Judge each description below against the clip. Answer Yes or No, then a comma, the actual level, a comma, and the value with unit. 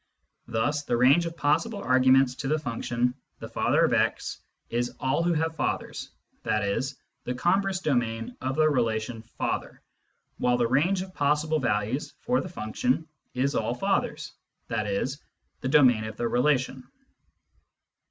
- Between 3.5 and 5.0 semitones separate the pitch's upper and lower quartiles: Yes, average, 4.7 semitones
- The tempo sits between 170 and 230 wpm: No, average, 155 wpm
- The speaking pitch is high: No, low, 130 Hz